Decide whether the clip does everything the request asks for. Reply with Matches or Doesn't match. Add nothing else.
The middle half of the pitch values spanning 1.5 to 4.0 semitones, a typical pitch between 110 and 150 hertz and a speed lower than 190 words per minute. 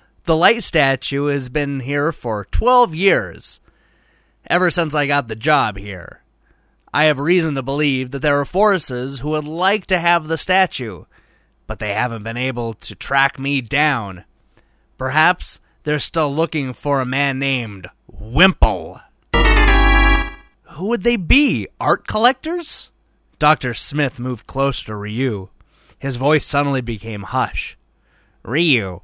Doesn't match